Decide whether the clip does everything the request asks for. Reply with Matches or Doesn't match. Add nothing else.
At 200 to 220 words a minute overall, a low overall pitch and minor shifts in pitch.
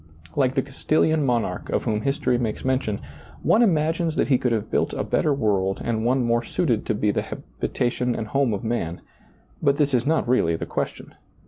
Doesn't match